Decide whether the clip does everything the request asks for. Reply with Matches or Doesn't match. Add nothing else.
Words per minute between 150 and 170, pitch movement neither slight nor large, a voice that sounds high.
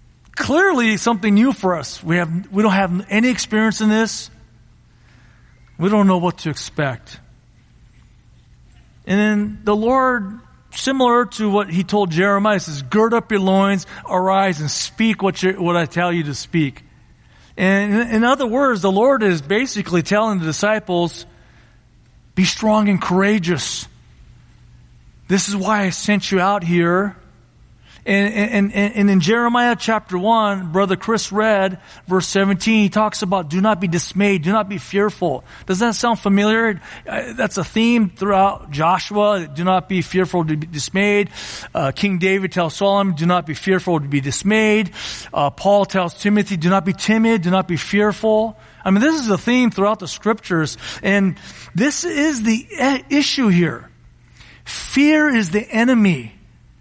Matches